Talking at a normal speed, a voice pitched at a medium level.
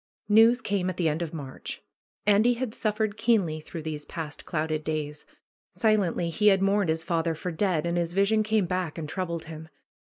Yes: average, 190 wpm; medium, 175 Hz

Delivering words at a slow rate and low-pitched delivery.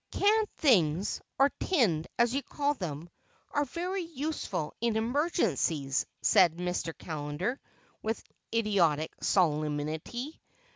No: slow, 95 wpm; high, 210 Hz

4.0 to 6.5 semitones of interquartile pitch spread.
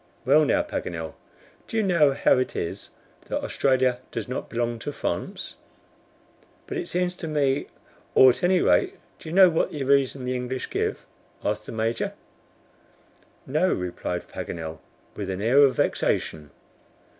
Yes: wide, 5.4 semitones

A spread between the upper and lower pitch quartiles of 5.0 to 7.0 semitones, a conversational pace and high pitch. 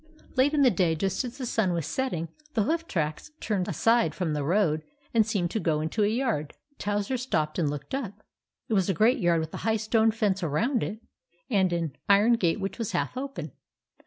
No: wide, 5.5 semitones; fast, 215 wpm; high, 200 Hz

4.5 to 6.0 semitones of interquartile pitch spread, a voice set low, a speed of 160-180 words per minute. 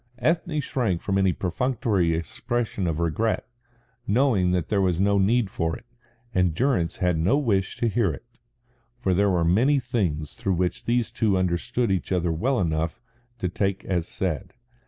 Yes: average, 5.2 semitones; very low, 95 Hz; average, 165 wpm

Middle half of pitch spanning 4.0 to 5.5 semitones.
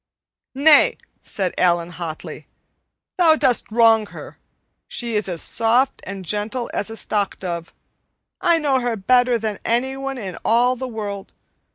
Yes: average, 4.4 semitones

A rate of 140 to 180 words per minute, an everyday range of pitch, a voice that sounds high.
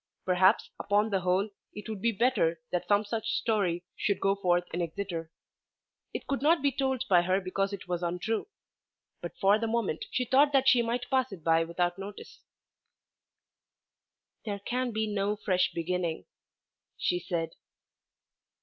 Yes: average, 160 wpm; average, 4.4 semitones; high, 200 Hz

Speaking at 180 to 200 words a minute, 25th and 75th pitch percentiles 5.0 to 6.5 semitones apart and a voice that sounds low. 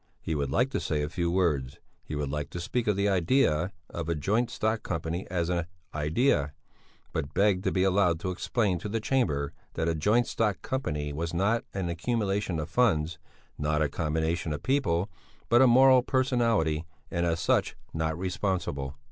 Yes: average, 185 wpm; wide, 5.4 semitones; very low, 85 Hz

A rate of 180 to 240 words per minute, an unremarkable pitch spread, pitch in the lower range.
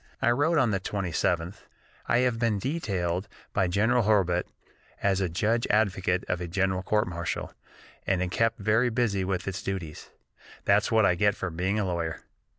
No: average, 170 wpm; average, 3.6 semitones; low, 100 Hz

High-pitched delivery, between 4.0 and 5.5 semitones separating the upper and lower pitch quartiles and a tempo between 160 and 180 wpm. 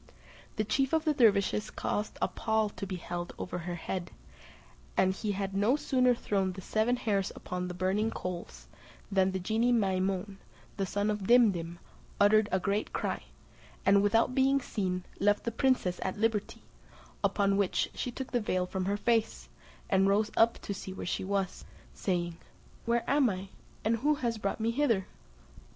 No: high, 205 Hz; average, 3.4 semitones; average, 170 wpm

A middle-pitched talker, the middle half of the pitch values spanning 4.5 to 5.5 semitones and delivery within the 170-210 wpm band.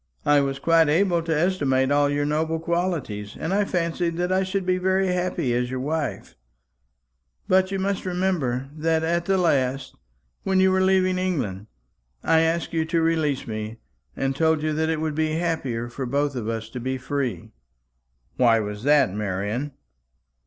Yes: medium, 155 Hz; average, 5.2 semitones; average, 175 wpm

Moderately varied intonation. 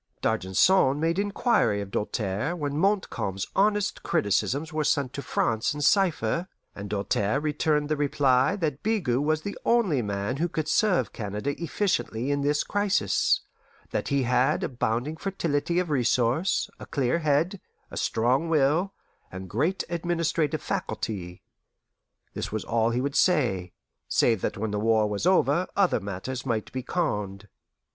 No: wide, 7.2 semitones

